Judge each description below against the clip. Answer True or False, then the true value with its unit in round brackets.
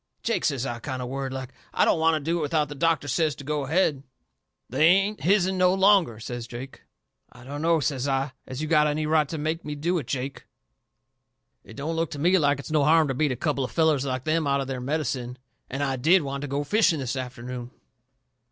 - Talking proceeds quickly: True (235 wpm)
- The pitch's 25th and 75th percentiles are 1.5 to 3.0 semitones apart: False (3.4 semitones)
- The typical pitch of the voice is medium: True (145 Hz)